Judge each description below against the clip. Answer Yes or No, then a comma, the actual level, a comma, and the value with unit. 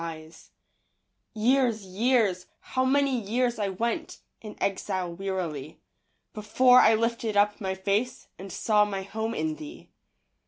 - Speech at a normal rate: No, slow, 125 wpm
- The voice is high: Yes, high, 215 Hz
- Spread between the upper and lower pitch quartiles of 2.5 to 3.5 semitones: No, average, 4.2 semitones